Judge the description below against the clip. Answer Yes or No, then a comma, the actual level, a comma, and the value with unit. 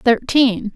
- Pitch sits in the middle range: No, high, 235 Hz